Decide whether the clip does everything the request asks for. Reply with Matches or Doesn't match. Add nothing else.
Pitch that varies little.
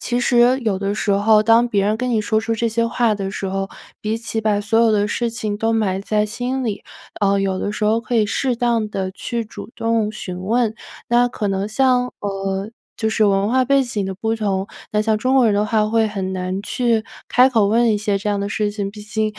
Matches